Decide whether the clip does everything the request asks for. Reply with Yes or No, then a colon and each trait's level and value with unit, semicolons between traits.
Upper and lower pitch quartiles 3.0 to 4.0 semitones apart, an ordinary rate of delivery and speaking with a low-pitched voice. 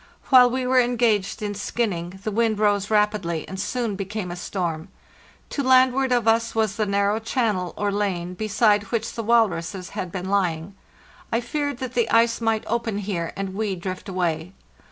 No: average, 3.6 semitones; average, 175 wpm; high, 210 Hz